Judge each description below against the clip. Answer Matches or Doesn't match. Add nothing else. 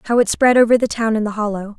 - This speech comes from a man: Doesn't match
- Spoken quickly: Matches